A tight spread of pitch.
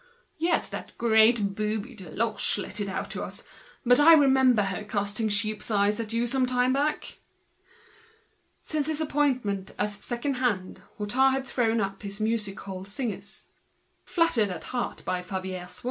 No: average, 4.2 semitones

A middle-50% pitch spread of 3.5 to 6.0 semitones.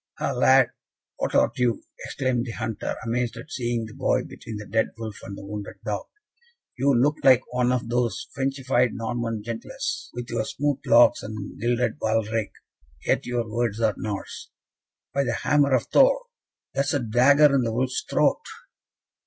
No: average, 2.9 semitones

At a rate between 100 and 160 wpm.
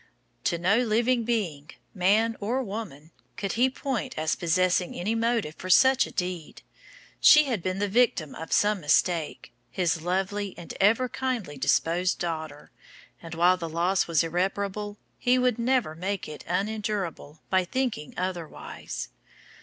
Yes: average, 145 wpm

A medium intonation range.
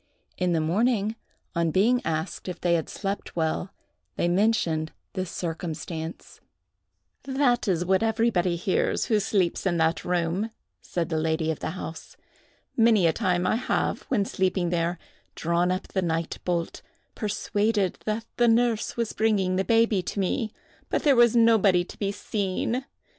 Yes: average, 4.4 semitones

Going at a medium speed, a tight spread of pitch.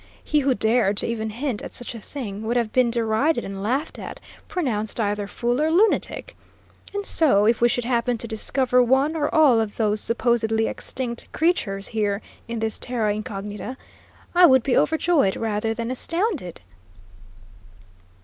No: average, 165 wpm; average, 4.0 semitones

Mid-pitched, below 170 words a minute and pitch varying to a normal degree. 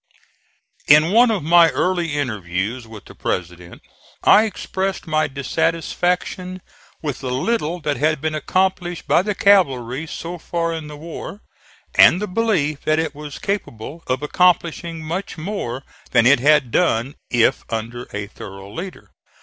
No: medium, 155 Hz; average, 150 wpm; wide, 5.8 semitones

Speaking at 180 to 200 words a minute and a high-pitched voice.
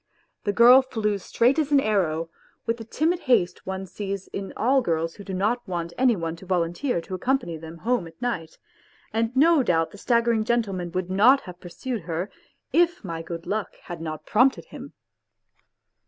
Yes: average, 185 wpm; high, 200 Hz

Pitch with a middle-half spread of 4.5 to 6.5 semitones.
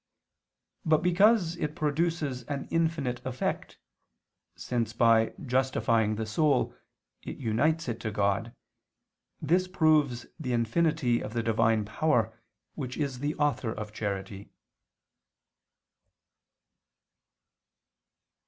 Yes: wide, 5.6 semitones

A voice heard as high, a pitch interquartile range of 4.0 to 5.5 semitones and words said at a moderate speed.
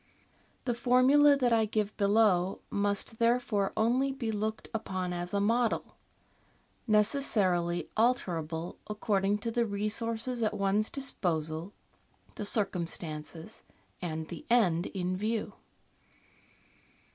No: high, 210 Hz; average, 4.3 semitones; slow, 110 wpm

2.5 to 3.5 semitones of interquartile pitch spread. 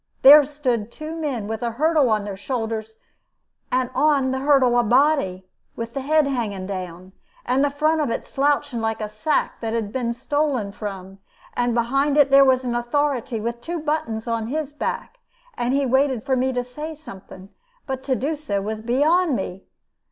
No: average, 4.5 semitones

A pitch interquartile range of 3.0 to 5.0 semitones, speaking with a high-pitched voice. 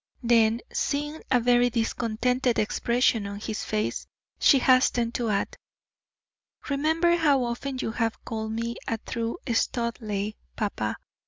No: narrow, 2.4 semitones; high, 235 Hz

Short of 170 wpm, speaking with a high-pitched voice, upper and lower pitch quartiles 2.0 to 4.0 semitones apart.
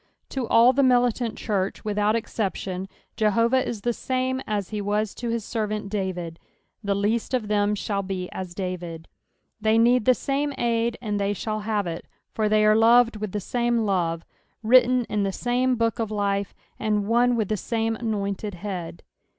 No: average, 185 wpm; high, 215 Hz; average, 2.8 semitones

